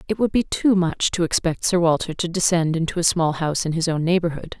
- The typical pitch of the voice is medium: Yes, medium, 170 Hz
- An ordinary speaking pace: No, fast, 250 wpm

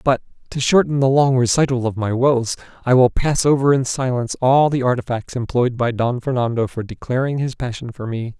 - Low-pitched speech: Yes, low, 125 Hz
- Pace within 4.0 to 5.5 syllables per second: No, 5.7 syllables/s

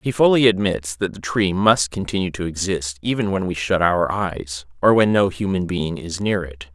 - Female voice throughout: No, male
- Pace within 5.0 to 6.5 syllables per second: No, 4.8 syllables/s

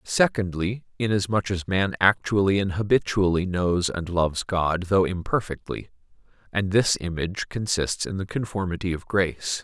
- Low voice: Yes, very low, 95 Hz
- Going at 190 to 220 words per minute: No, slow, 135 wpm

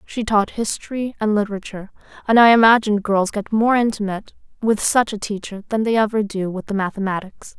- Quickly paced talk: No, average, 180 wpm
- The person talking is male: No, female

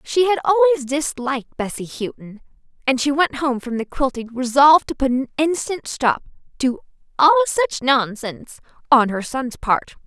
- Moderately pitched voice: No, very high, 275 Hz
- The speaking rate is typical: Yes, average, 160 wpm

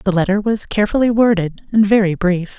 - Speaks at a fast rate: No, average, 185 wpm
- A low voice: No, high, 200 Hz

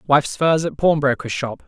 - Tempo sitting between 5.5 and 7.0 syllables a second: No, 4.9 syllables/s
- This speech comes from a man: Yes, male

